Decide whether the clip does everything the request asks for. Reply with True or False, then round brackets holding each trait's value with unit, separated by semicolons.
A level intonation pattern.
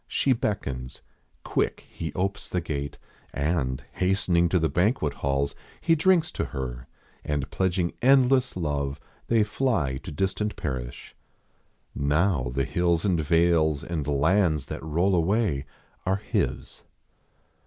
False (5.5 semitones)